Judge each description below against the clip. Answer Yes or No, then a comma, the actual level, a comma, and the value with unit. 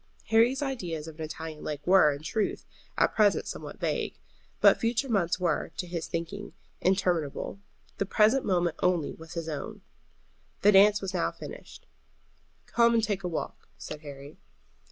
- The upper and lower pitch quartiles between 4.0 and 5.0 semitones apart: Yes, average, 4.5 semitones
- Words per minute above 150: Yes, average, 160 wpm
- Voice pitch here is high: No, medium, 180 Hz